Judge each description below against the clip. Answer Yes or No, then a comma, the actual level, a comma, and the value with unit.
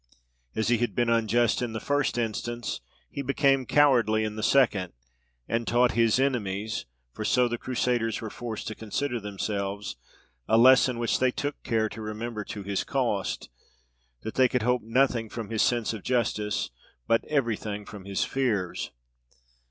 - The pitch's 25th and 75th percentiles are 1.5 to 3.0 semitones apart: Yes, narrow, 2.6 semitones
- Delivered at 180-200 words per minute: No, average, 165 wpm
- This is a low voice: Yes, low, 115 Hz